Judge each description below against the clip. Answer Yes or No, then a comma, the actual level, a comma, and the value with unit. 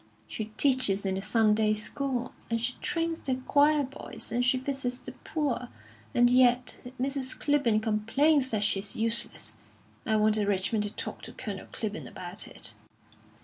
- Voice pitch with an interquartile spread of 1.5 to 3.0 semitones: No, average, 3.9 semitones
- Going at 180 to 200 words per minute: No, average, 155 wpm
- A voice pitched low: No, high, 240 Hz